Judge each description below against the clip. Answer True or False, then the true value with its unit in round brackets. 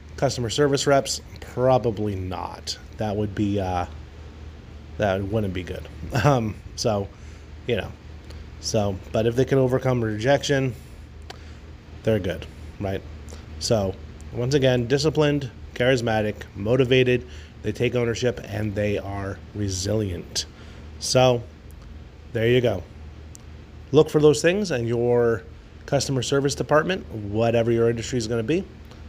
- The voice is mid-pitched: False (105 Hz)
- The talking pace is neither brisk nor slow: False (125 wpm)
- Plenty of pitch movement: True (7.8 semitones)